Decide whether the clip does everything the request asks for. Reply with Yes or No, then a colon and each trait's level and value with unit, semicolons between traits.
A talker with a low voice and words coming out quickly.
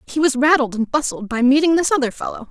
No: very high, 275 Hz; fast, 240 wpm